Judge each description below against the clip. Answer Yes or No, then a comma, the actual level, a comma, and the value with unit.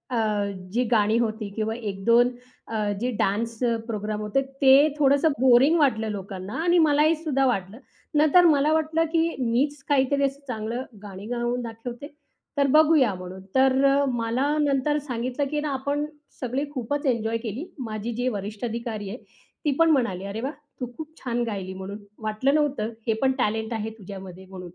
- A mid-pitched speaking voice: No, high, 240 Hz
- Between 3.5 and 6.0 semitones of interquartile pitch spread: Yes, average, 4.7 semitones